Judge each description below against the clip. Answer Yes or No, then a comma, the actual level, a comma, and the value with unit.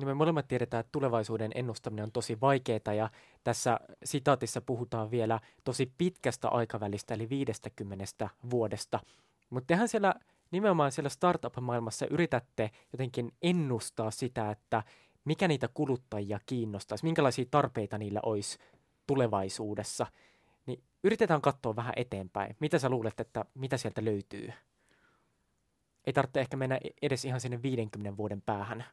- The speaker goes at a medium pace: Yes, average, 130 wpm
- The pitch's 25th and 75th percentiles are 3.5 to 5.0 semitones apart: Yes, average, 3.9 semitones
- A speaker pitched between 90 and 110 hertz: No, low, 120 Hz